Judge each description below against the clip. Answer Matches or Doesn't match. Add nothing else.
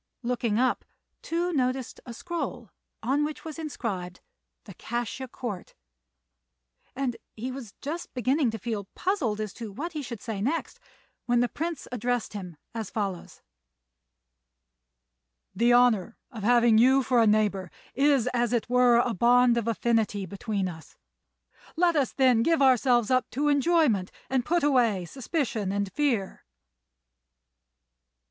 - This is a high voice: Matches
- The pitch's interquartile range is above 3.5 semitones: Matches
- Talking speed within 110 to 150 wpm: Matches